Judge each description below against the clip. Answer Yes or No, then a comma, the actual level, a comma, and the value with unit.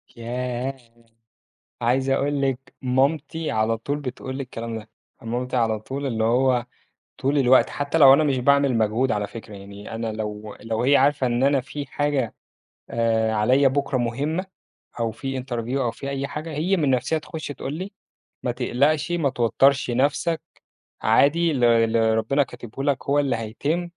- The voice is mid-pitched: No, low, 130 Hz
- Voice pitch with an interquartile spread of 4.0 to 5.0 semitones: No, average, 3.5 semitones